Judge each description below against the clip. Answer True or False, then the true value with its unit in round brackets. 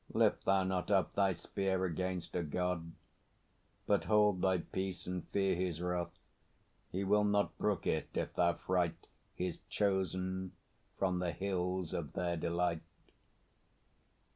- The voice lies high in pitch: False (90 Hz)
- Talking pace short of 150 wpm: True (140 wpm)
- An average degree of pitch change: False (1.5 semitones)